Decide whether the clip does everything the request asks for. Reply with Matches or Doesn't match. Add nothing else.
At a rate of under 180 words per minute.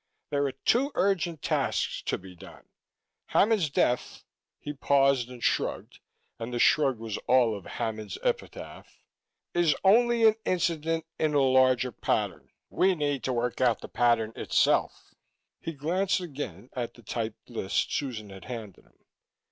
Matches